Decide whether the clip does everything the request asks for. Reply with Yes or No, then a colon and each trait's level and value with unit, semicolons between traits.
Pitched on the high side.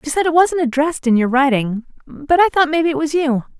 Yes: very high, 290 Hz